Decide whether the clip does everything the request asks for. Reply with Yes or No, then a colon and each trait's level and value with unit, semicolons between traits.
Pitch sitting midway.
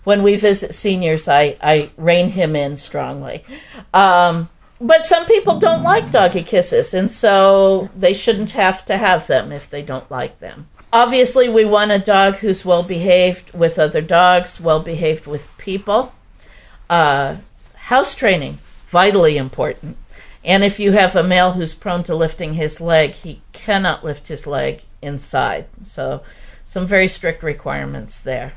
Yes: medium, 180 Hz